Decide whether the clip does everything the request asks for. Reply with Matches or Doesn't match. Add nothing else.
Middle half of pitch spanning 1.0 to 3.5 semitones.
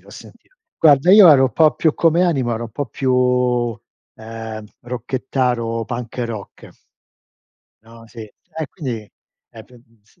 Doesn't match